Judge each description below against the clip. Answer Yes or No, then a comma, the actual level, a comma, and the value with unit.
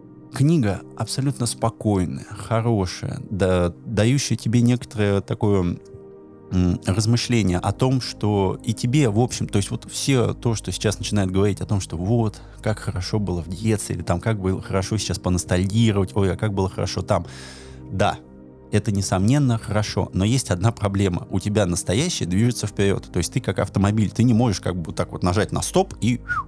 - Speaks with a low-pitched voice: Yes, low, 105 Hz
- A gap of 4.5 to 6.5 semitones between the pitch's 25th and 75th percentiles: No, average, 3.7 semitones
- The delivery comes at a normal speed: No, fast, 175 wpm